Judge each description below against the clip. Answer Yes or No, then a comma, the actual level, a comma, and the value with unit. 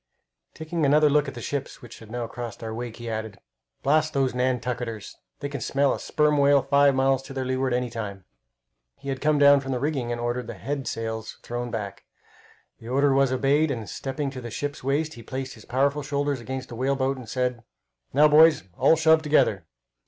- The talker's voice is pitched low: Yes, low, 130 Hz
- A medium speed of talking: No, fast, 210 wpm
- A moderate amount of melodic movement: Yes, average, 3.0 semitones